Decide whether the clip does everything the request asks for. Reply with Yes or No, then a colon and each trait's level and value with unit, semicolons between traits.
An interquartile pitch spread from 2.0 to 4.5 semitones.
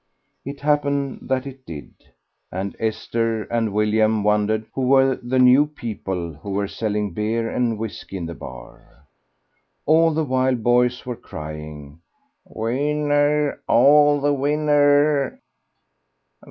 No: average, 5.3 semitones